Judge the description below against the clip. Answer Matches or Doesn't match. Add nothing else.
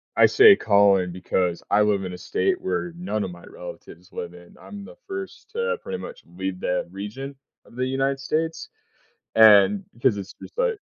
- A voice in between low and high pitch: Doesn't match